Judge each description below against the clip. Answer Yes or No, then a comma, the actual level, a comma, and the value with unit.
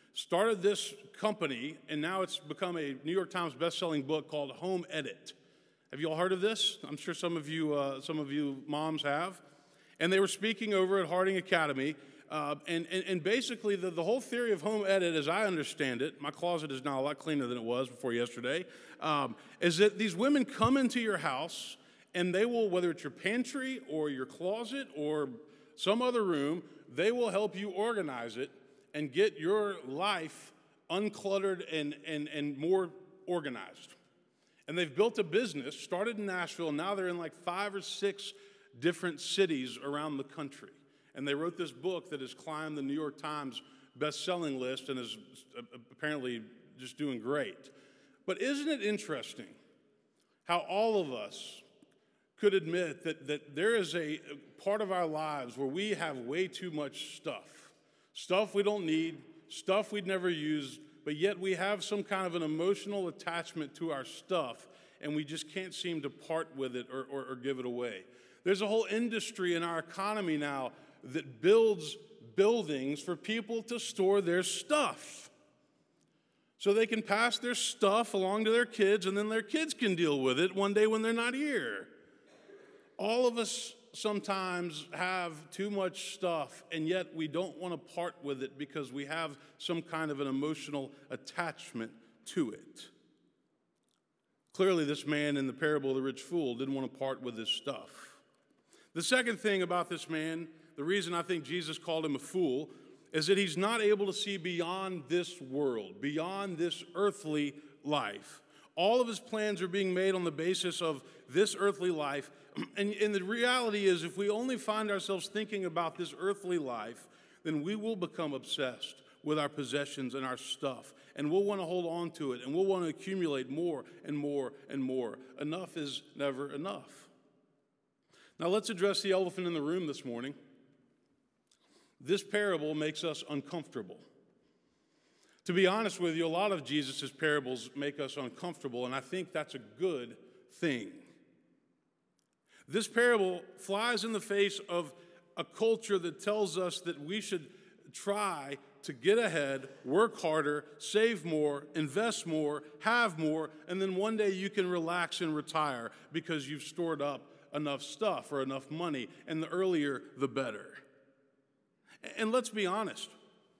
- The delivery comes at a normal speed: Yes, average, 175 wpm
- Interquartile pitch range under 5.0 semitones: No, average, 5.3 semitones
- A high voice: No, medium, 170 Hz